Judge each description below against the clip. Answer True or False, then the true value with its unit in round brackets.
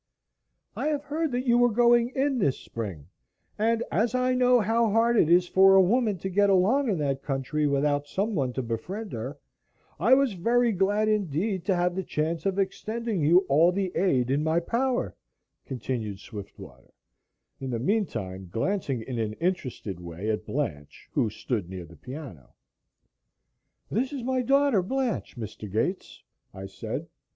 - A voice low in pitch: False (180 Hz)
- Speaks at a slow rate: False (165 wpm)